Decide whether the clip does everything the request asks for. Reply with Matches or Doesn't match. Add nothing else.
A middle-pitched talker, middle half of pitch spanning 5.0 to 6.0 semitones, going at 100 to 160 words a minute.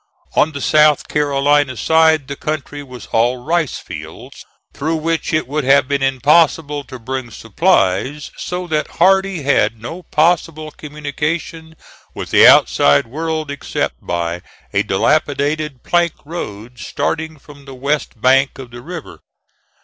Doesn't match